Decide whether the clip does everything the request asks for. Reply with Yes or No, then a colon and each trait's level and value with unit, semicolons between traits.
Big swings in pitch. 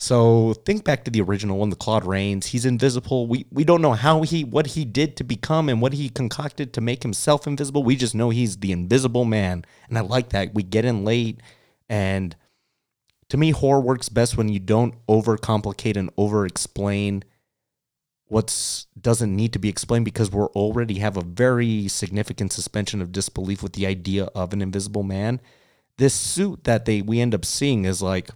No: average, 4.1 semitones